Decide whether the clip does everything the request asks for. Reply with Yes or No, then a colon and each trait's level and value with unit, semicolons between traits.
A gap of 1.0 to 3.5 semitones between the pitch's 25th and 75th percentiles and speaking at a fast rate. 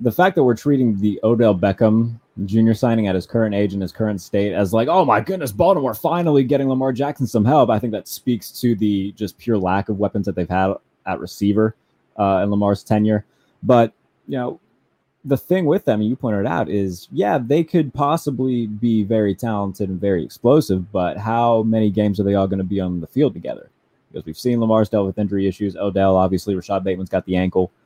Yes: average, 3.0 semitones; fast, 220 wpm